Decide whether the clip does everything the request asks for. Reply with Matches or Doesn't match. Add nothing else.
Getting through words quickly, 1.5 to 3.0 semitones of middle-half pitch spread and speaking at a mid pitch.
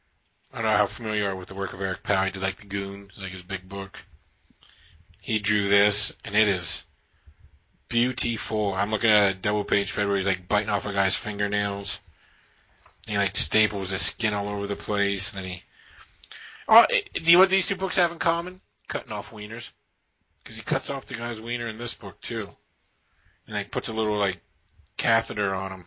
Doesn't match